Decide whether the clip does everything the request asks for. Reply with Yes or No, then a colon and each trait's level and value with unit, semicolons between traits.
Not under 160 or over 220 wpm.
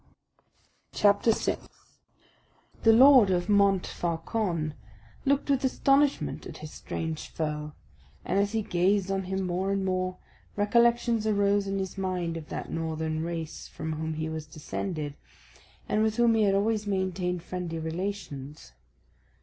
No: average, 140 wpm